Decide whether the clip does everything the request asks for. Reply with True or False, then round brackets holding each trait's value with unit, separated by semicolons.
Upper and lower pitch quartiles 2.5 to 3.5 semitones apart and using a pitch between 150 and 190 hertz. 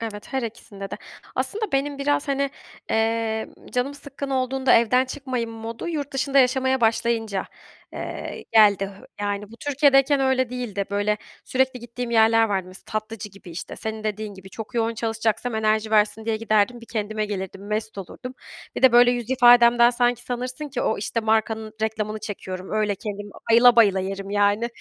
False (3.0 semitones; 225 Hz)